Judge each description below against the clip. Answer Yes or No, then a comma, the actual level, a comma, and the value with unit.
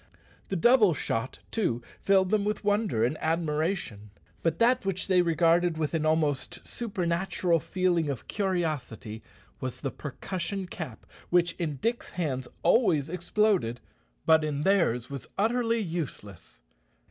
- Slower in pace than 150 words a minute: Yes, slow, 135 wpm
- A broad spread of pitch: No, average, 5.0 semitones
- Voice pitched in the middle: Yes, medium, 170 Hz